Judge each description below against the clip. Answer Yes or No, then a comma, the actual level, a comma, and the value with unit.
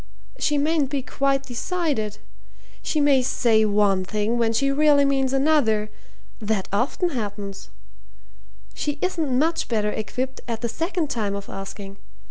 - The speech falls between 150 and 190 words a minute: No, average, 140 wpm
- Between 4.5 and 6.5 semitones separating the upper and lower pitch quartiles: Yes, wide, 5.4 semitones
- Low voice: No, very high, 250 Hz